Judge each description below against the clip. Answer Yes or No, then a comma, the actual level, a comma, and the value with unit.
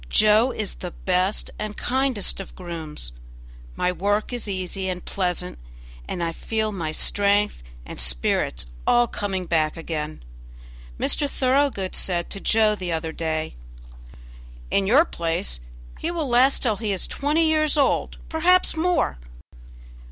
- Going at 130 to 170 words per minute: Yes, average, 140 wpm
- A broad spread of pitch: Yes, wide, 6.4 semitones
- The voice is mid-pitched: No, high, 200 Hz